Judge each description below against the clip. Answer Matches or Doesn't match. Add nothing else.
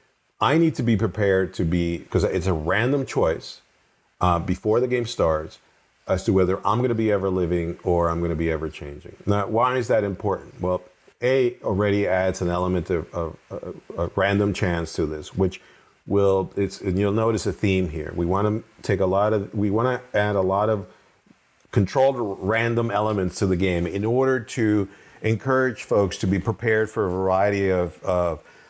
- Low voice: Matches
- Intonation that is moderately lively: Matches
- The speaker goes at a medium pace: Matches